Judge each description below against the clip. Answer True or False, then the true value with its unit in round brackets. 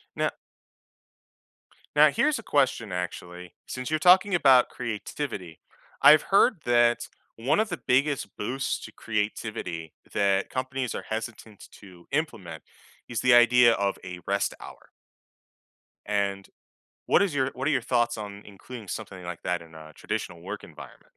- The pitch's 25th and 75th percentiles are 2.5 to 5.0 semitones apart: False (5.4 semitones)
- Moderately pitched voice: False (115 Hz)